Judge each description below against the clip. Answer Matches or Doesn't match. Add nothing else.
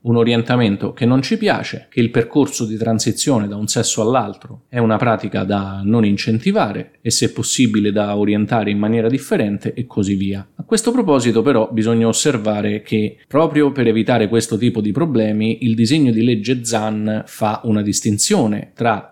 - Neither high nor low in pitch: Doesn't match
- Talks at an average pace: Doesn't match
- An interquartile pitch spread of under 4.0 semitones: Matches